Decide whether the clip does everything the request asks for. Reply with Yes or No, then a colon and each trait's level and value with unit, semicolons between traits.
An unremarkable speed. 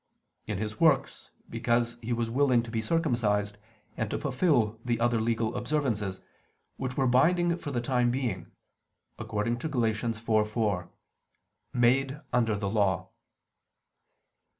No: slow, 130 wpm